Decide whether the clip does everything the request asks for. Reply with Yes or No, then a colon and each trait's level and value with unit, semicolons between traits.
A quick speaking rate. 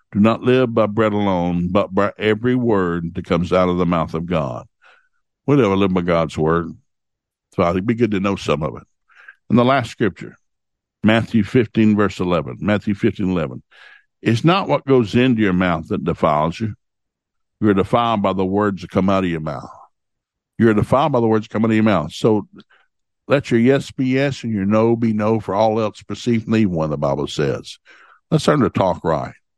Yes: fast, 210 wpm